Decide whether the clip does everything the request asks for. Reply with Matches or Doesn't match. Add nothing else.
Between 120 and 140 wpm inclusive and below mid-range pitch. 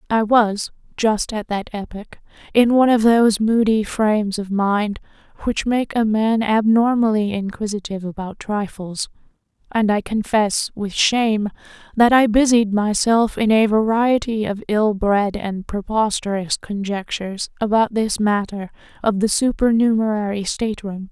Doesn't match